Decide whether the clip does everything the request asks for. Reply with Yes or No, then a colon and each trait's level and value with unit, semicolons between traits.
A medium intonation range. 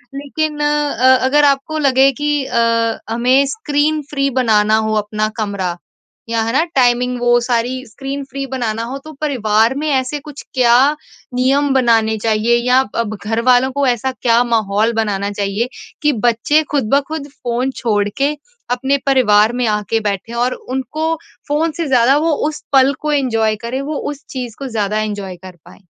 Yes: average, 3.9 semitones